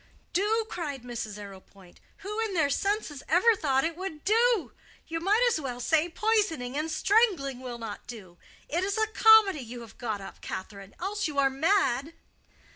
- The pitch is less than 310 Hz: No, very high, 315 Hz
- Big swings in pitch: Yes, wide, 8.6 semitones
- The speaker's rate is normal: Yes, average, 175 wpm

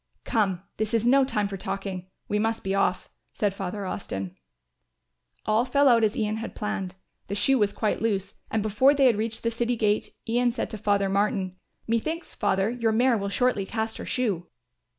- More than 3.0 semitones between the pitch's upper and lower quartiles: No, average, 2.7 semitones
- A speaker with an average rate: Yes, average, 190 wpm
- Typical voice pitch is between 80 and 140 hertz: No, high, 215 Hz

